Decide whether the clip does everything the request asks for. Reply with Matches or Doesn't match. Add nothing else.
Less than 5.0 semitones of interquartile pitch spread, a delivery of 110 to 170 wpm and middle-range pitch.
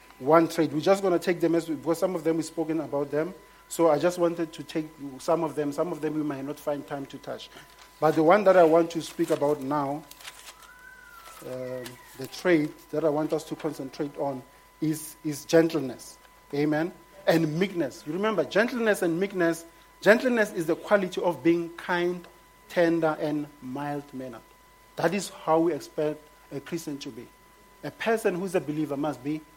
Doesn't match